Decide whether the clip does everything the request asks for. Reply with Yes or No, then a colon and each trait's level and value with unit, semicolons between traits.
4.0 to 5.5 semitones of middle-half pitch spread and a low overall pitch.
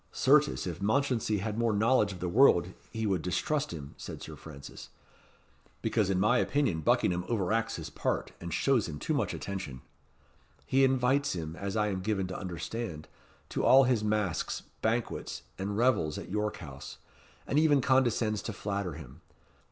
Yes: average, 5.2 semitones; low, 105 Hz